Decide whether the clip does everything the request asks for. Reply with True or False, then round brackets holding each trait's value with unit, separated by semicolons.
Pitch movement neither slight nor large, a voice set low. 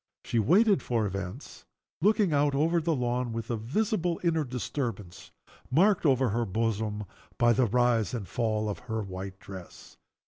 False (5.9 semitones; 120 Hz)